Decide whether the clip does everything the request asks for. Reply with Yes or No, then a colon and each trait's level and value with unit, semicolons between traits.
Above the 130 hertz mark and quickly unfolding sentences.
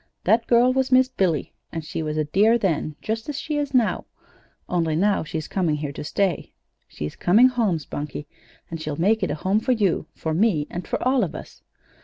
Yes: high, 190 Hz; fast, 210 wpm